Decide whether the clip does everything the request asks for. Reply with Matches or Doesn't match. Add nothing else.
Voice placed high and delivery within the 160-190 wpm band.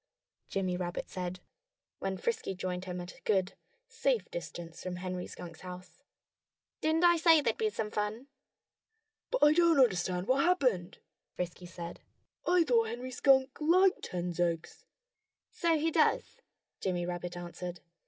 Doesn't match